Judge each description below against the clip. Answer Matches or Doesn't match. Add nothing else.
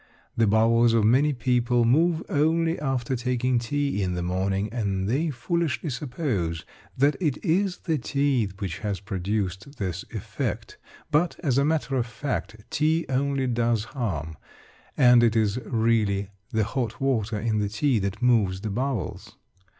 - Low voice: Matches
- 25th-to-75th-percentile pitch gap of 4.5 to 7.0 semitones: Matches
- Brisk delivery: Doesn't match